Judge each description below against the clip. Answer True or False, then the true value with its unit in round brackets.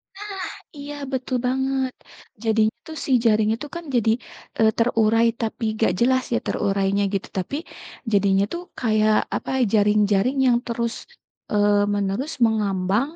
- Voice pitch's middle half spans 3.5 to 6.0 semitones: True (3.8 semitones)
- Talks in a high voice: True (220 Hz)